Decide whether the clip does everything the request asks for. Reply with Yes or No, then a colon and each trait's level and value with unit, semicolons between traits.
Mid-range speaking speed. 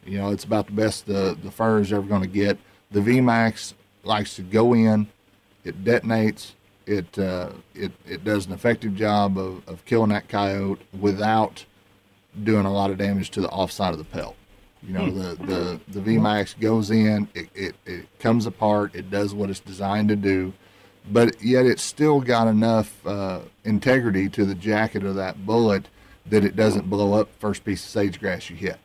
Yes: average, 195 wpm